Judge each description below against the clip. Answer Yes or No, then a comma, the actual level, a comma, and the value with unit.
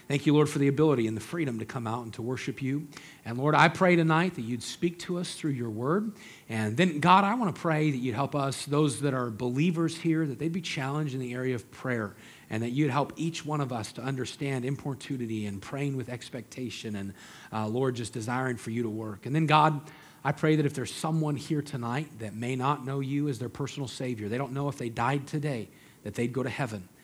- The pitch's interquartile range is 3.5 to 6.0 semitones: Yes, average, 4.0 semitones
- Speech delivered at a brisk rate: Yes, fast, 245 wpm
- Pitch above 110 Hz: Yes, low, 135 Hz